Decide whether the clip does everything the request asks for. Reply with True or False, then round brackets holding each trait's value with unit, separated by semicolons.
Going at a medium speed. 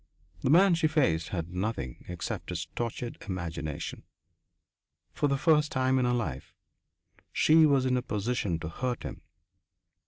True (150 wpm)